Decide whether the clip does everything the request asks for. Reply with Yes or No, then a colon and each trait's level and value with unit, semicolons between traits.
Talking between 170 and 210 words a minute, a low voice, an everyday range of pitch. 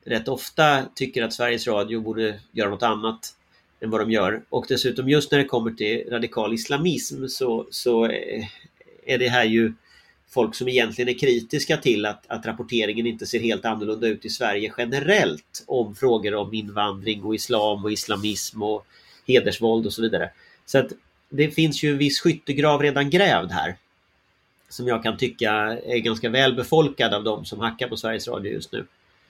Yes: average, 175 wpm; low, 115 Hz; average, 3.5 semitones